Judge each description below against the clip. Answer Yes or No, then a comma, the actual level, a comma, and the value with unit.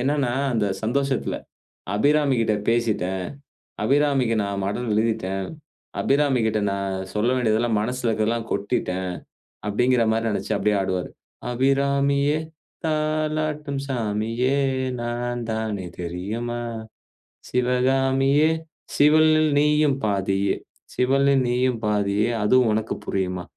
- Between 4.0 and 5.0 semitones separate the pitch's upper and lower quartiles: Yes, average, 4.7 semitones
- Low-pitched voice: Yes, low, 120 Hz